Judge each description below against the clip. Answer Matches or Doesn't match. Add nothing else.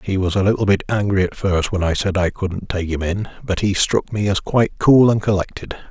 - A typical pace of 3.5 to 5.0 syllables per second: Doesn't match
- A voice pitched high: Doesn't match